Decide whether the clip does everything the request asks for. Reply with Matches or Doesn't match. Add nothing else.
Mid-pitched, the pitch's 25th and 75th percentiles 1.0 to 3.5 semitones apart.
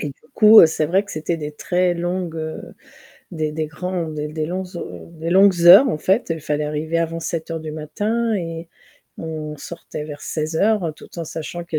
Matches